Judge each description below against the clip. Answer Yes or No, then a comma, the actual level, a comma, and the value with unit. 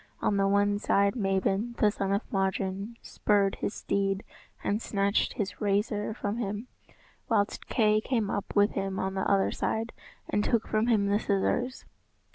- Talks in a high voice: Yes, high, 205 Hz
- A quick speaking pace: No, average, 165 wpm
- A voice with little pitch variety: Yes, narrow, 1.5 semitones